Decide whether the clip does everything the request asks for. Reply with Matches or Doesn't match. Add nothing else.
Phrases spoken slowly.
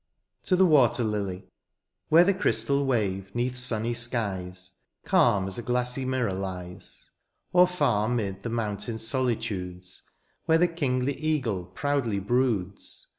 Matches